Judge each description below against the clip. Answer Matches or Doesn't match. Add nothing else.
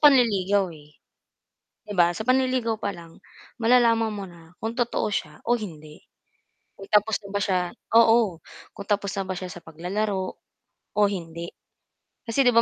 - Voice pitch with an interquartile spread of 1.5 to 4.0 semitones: Doesn't match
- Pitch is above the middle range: Matches